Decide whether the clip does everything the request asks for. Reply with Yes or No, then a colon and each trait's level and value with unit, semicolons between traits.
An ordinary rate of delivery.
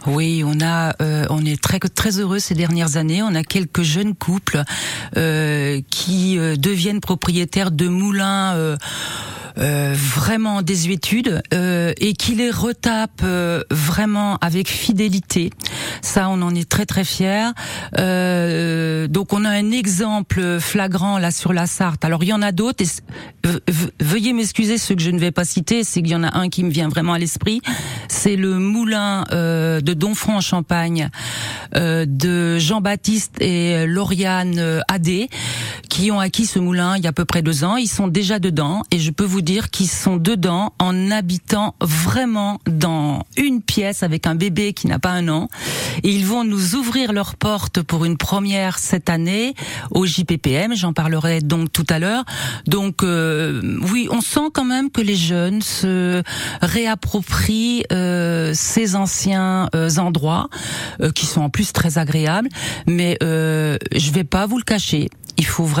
Yes: average, 170 wpm